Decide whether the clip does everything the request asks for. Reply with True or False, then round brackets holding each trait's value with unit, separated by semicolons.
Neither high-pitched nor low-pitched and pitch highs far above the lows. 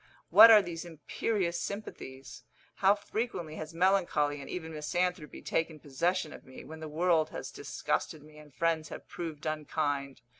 False (160 Hz; 2.9 semitones)